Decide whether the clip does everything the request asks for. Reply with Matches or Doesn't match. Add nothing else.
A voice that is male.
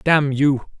Matches